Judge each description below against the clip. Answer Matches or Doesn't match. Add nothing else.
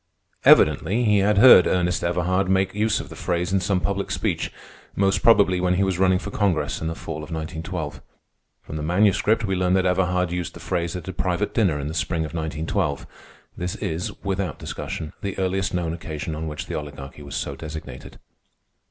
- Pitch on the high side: Doesn't match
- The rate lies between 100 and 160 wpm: Doesn't match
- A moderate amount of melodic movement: Matches